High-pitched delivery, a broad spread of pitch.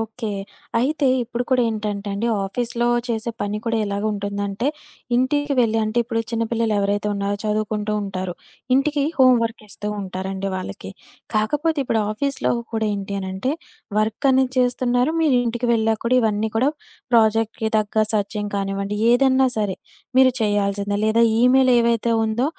No: high, 220 Hz; average, 3.2 semitones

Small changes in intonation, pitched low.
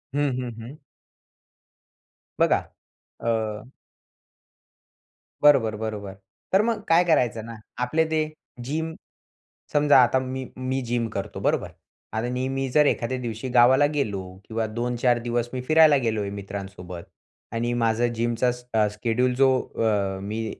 No: average, 3.3 semitones; low, 120 Hz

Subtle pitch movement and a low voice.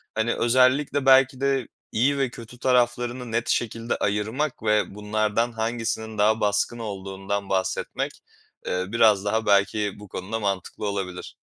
No: average, 3.0 semitones; low, 110 Hz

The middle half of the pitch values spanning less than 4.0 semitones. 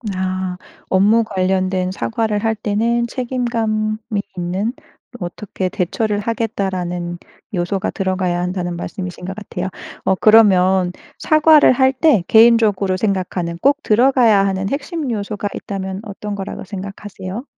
Yes: average, 3.3 semitones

